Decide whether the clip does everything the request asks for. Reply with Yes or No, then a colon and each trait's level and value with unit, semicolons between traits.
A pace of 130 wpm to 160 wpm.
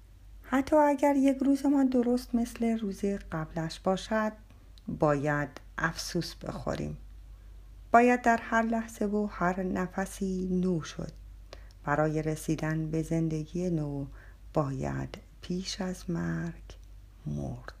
No: average, 110 wpm